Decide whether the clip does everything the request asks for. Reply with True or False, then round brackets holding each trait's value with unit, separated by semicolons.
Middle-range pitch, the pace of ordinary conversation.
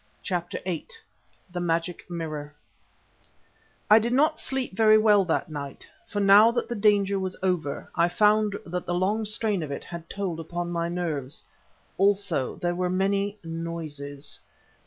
True (180 Hz; 155 wpm)